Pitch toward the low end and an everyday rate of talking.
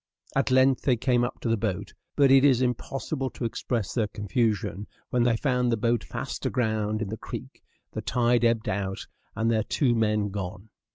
Yes: low, 115 Hz; average, 190 wpm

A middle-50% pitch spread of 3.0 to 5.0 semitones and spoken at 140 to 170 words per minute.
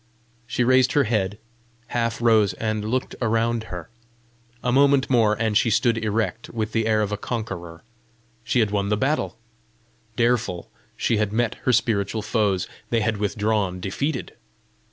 No: narrow, 2.4 semitones; average, 155 wpm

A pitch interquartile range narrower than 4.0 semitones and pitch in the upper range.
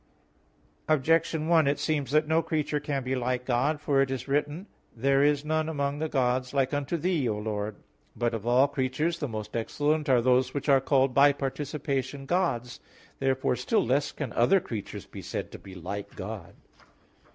No: average, 3.1 semitones; low, 135 Hz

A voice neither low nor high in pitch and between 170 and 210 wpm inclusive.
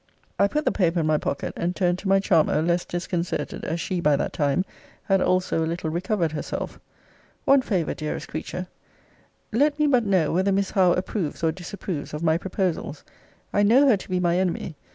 Yes: medium, 180 Hz; average, 195 wpm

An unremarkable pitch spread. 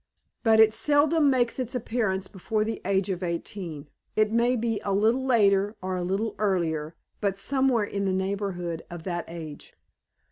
Yes: average, 3.7 semitones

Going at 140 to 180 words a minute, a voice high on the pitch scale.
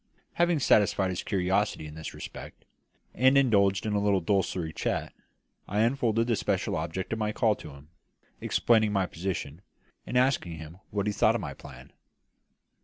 No: average, 170 wpm; low, 100 Hz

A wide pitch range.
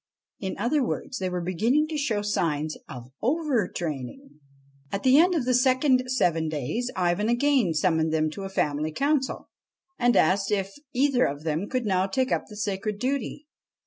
Yes: wide, 7.3 semitones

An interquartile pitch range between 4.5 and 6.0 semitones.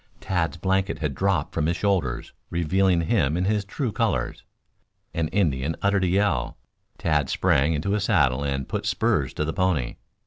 Yes: average, 5.0 semitones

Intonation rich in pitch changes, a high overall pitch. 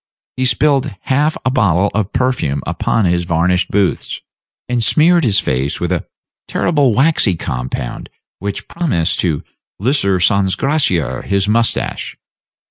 No: wide, 7.1 semitones; low, 100 Hz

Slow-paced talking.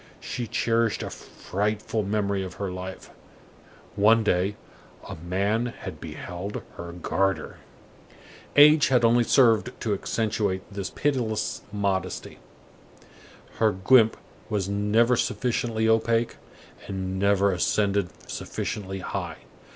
Yes: slow, 110 wpm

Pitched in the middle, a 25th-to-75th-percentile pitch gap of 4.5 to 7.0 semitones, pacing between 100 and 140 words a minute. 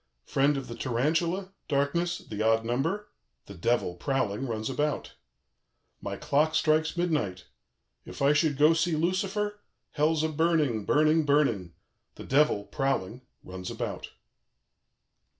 Yes: medium, 145 Hz; wide, 5.6 semitones; slow, 135 wpm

